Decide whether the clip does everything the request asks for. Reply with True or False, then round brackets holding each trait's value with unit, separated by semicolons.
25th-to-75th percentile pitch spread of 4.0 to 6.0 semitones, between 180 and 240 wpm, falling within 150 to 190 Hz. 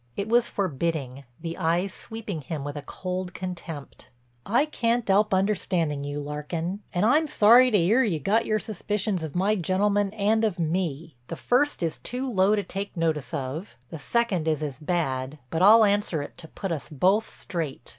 True (5.1 semitones; 185 wpm; 185 Hz)